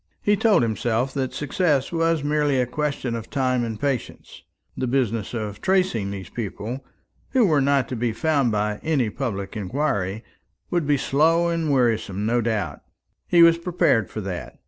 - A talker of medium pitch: No, low, 130 Hz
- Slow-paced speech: No, average, 170 wpm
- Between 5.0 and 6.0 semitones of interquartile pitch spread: Yes, wide, 5.4 semitones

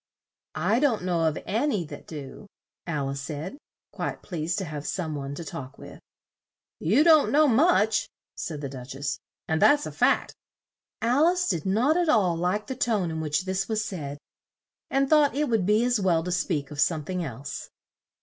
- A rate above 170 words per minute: Yes, average, 195 wpm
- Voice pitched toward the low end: No, medium, 185 Hz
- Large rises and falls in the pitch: Yes, wide, 7.7 semitones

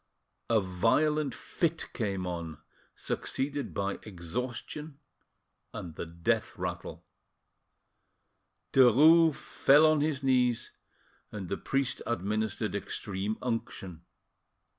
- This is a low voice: Yes, low, 115 Hz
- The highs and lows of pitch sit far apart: Yes, wide, 6.3 semitones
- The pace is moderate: No, slow, 95 wpm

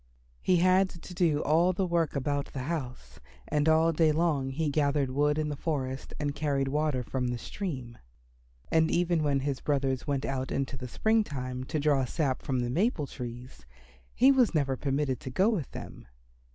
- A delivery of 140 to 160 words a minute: No, average, 190 wpm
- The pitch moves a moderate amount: Yes, average, 3.6 semitones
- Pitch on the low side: No, medium, 145 Hz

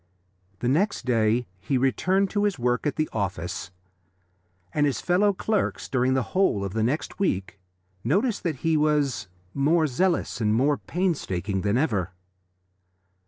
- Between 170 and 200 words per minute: No, average, 150 wpm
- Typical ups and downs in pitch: No, wide, 7.7 semitones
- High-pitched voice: No, low, 135 Hz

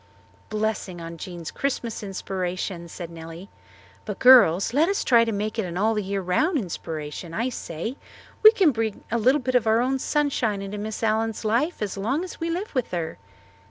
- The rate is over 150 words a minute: Yes, average, 190 wpm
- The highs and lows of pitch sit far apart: Yes, wide, 5.7 semitones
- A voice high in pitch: Yes, high, 215 Hz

